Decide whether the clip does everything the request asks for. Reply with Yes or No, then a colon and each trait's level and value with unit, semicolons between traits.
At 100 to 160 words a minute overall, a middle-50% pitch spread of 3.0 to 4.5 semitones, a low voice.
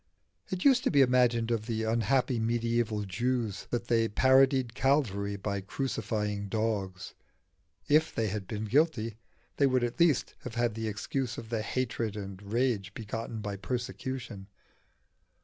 Yes: average, 150 wpm; average, 3.5 semitones; low, 115 Hz